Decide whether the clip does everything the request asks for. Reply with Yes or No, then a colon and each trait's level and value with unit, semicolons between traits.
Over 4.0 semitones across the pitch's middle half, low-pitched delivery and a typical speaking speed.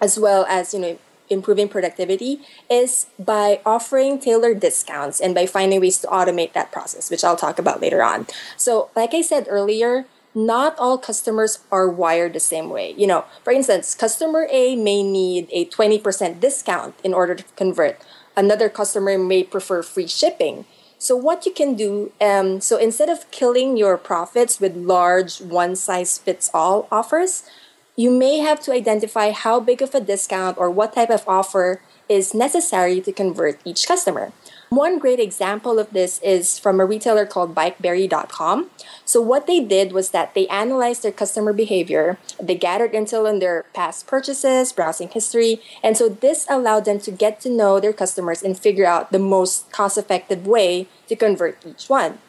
No: average, 4.6 semitones; high, 210 Hz; average, 175 wpm